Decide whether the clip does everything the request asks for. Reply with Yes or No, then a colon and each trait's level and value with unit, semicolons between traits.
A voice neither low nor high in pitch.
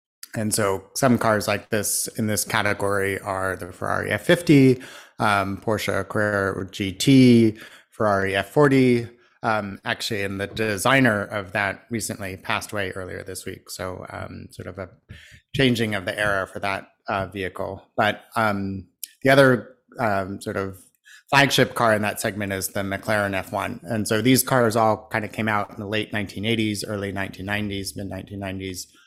No: low, 105 Hz